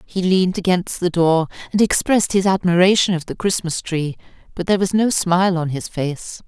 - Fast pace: No, average, 195 wpm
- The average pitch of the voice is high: No, medium, 180 Hz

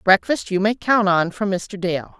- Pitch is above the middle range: Yes, high, 195 Hz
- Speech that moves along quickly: Yes, fast, 220 wpm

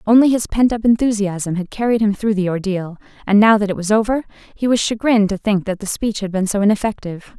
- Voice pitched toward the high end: Yes, high, 210 Hz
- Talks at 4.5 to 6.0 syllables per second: No, 6.2 syllables/s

